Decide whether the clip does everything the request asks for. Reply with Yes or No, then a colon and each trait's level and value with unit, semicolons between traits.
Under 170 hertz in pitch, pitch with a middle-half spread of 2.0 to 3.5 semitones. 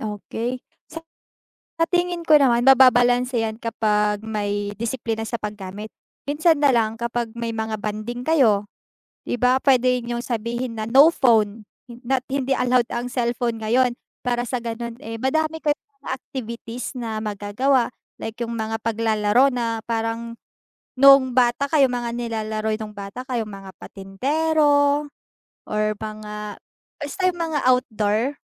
No: high, 235 Hz; average, 3.1 semitones